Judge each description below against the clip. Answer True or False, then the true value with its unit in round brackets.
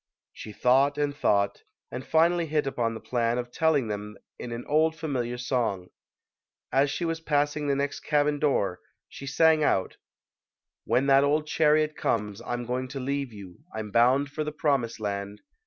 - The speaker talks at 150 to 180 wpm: True (170 wpm)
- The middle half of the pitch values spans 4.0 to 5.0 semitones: True (4.3 semitones)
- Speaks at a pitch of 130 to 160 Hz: True (135 Hz)